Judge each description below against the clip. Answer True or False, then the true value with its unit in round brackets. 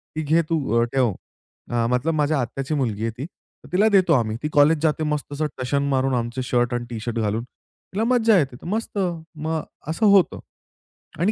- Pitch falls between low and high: True (145 Hz)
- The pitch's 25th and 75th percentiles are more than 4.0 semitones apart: True (5.0 semitones)